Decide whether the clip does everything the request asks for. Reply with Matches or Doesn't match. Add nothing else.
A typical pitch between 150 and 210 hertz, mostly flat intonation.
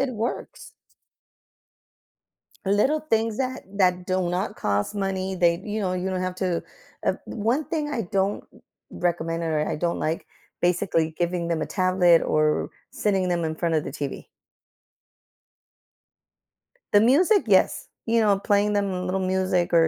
Doesn't match